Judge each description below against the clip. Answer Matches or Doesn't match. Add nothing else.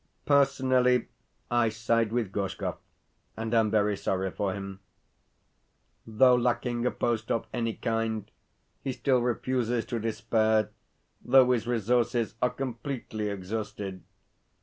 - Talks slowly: Matches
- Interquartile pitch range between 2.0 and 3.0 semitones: Matches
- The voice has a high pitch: Doesn't match